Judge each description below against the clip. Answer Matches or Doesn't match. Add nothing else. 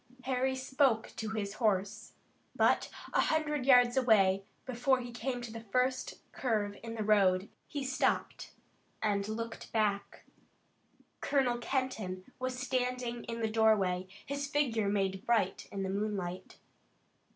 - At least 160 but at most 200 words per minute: Doesn't match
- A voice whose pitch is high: Matches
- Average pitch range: Matches